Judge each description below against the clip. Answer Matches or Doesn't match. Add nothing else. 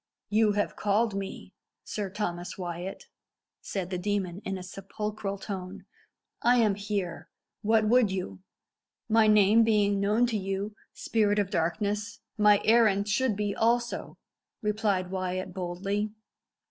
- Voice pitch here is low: Doesn't match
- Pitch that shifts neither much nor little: Doesn't match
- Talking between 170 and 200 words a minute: Doesn't match